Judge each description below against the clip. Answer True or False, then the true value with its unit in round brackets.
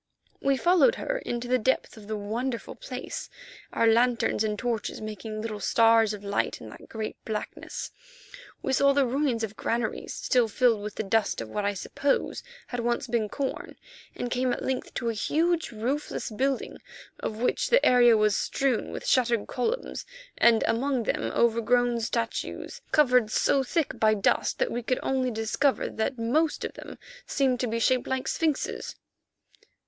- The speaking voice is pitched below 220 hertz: False (240 Hz)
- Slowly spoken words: False (170 wpm)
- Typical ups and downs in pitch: True (3.1 semitones)